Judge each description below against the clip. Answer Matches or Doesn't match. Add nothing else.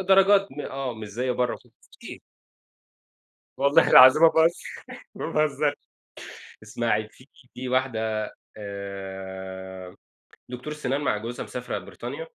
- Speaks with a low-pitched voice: Matches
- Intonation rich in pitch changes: Matches